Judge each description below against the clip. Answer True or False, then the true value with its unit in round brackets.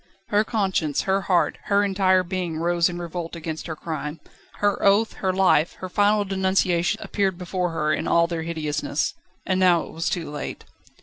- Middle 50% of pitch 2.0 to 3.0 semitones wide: True (2.6 semitones)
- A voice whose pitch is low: False (180 Hz)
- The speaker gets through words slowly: False (180 wpm)